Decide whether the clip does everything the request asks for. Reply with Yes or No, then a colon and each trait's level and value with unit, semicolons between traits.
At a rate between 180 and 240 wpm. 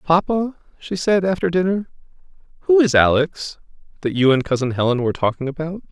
No: average, 160 wpm